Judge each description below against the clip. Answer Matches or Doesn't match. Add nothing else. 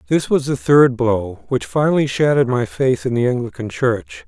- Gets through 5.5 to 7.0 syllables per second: Doesn't match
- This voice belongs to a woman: Doesn't match